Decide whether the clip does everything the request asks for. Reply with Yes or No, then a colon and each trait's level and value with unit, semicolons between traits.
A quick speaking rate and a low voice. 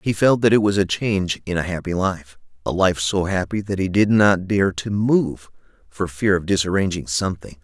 Yes: fast, 210 wpm; very low, 95 Hz